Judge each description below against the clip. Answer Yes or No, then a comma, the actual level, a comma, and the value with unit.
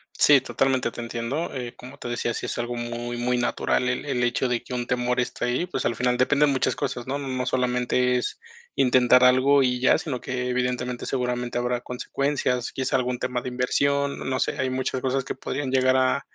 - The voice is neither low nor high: No, low, 125 Hz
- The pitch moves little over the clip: Yes, narrow, 1.2 semitones